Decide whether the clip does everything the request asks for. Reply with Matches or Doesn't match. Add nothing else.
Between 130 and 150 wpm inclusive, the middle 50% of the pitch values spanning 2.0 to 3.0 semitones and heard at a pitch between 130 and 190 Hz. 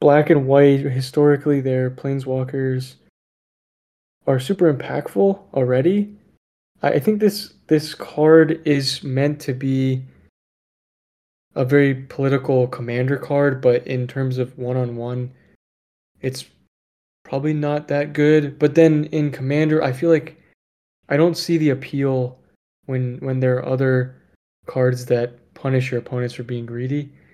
Matches